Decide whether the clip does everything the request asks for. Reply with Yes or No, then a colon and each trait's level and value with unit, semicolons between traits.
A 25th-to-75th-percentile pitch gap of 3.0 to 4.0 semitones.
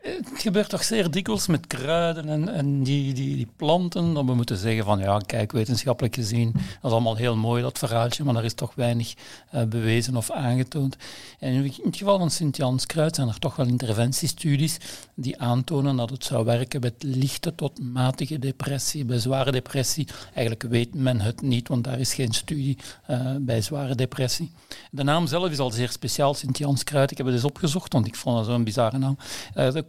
Yes: average, 3.4 semitones